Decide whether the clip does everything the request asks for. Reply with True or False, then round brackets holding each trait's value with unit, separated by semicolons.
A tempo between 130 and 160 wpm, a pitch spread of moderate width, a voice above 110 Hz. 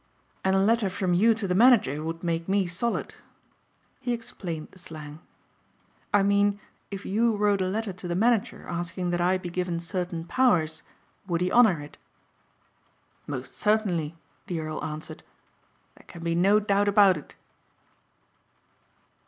True (155 wpm; 3.4 semitones; 185 Hz)